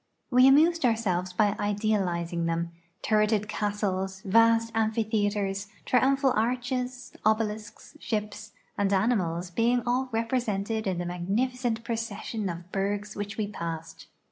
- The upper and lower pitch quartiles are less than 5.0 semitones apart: Yes, average, 3.0 semitones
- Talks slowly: Yes, slow, 115 wpm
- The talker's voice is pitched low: No, high, 210 Hz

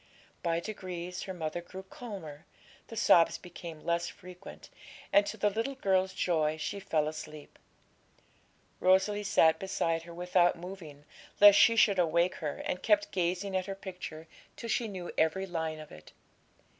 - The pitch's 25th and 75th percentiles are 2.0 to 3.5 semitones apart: Yes, average, 3.1 semitones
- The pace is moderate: Yes, average, 155 wpm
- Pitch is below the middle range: No, medium, 180 Hz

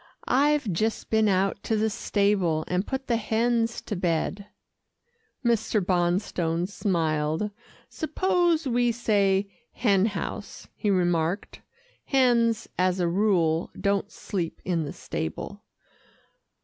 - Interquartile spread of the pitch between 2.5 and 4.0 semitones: No, average, 4.6 semitones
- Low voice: No, high, 200 Hz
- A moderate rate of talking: No, slow, 115 wpm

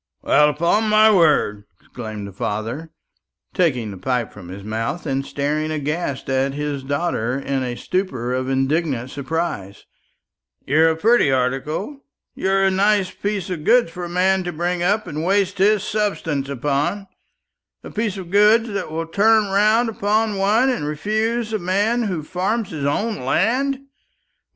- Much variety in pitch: Yes, wide, 6.9 semitones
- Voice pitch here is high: No, medium, 170 Hz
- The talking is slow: No, average, 160 wpm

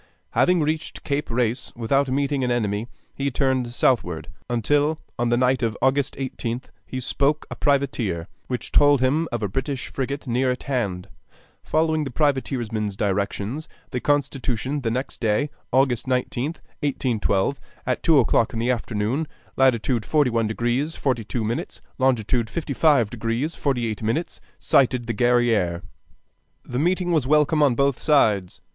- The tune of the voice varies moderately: Yes, average, 3.6 semitones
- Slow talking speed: No, average, 145 wpm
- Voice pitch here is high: No, low, 125 Hz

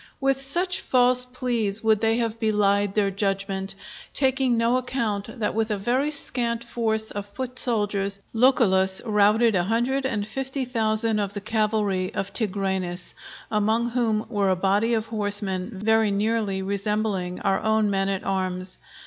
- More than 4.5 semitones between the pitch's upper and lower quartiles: No, average, 2.9 semitones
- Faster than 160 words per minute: No, average, 155 wpm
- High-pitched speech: Yes, high, 215 Hz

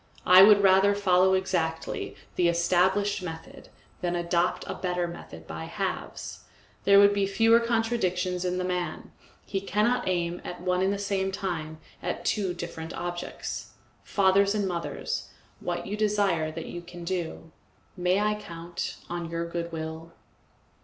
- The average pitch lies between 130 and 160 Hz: No, medium, 180 Hz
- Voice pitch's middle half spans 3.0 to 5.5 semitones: No, narrow, 2.6 semitones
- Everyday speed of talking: Yes, average, 150 wpm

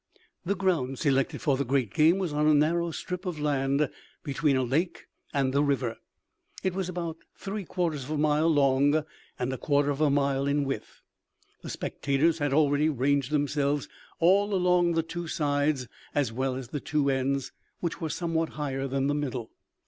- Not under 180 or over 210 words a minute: Yes, average, 185 wpm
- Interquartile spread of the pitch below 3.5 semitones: Yes, average, 3.1 semitones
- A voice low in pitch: No, medium, 145 Hz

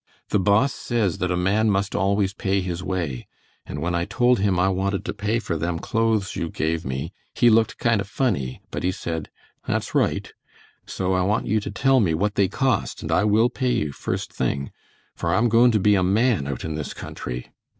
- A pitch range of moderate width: Yes, average, 4.2 semitones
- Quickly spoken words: Yes, fast, 215 wpm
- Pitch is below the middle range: Yes, very low, 95 Hz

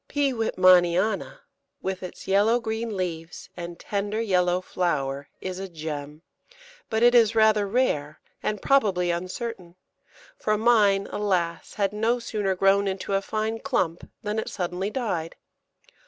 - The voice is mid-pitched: No, high, 195 Hz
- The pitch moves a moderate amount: Yes, average, 3.8 semitones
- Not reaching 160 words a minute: Yes, average, 140 wpm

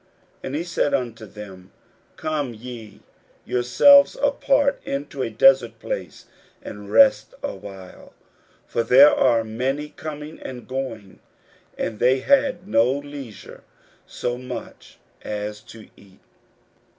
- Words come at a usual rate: No, slow, 125 wpm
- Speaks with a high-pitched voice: No, low, 125 Hz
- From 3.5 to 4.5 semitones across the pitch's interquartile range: No, average, 4.9 semitones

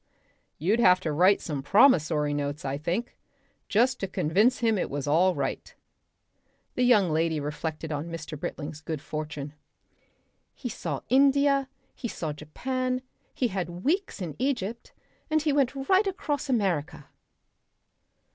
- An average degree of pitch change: No, wide, 8.7 semitones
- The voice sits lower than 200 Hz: Yes, medium, 185 Hz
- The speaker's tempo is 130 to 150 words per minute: Yes, average, 140 wpm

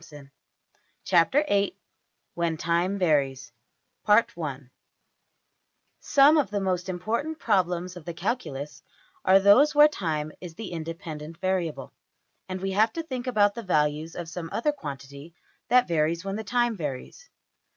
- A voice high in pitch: No, medium, 180 Hz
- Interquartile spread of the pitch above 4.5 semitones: Yes, average, 5.3 semitones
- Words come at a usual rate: No, slow, 130 wpm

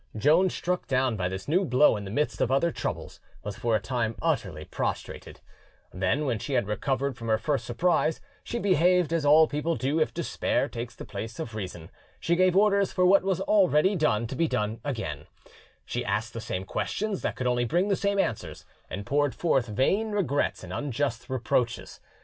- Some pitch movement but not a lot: No, wide, 7.2 semitones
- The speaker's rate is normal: Yes, average, 195 wpm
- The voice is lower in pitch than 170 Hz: Yes, low, 135 Hz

